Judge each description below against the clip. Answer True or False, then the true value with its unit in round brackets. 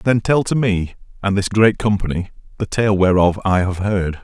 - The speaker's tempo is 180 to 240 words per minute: True (200 wpm)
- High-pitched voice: False (100 Hz)